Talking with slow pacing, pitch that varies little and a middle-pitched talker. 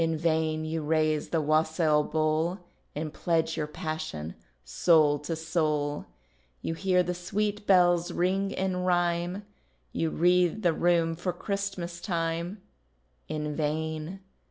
Yes: slow, 130 wpm; narrow, 2.3 semitones; medium, 165 Hz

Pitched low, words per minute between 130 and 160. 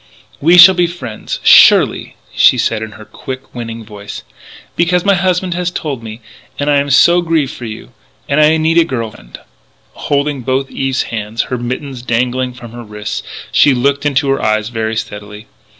No: low, 130 Hz; average, 185 wpm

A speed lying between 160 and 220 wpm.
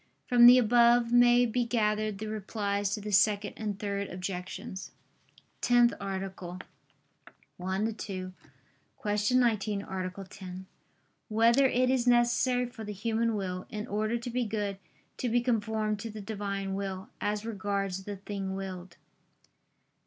No: average, 145 wpm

